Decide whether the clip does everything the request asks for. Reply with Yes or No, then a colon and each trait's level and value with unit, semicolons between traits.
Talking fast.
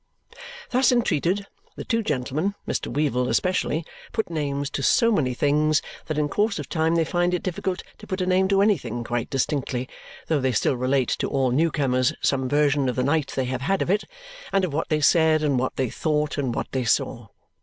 Yes: fast, 210 wpm